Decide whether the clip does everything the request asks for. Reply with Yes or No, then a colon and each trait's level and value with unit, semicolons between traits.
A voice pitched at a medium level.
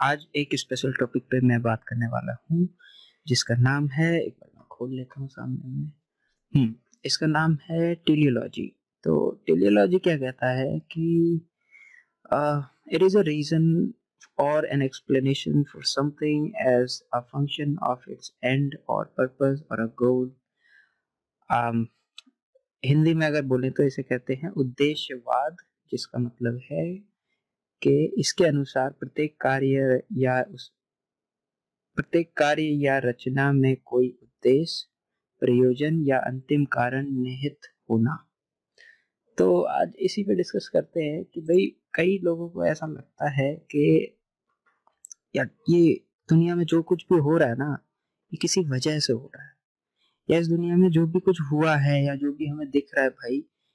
Yes: medium, 145 Hz